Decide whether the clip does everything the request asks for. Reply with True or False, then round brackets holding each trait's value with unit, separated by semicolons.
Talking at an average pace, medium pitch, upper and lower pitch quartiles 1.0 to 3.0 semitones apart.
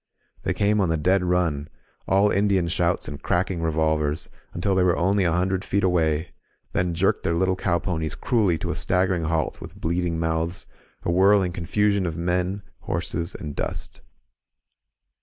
False (170 wpm; 90 Hz; 2.5 semitones)